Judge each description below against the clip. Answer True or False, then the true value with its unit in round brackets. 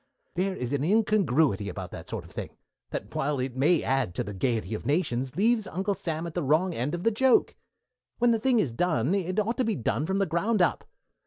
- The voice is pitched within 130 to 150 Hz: False (170 Hz)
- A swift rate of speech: True (230 wpm)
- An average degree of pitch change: False (7.4 semitones)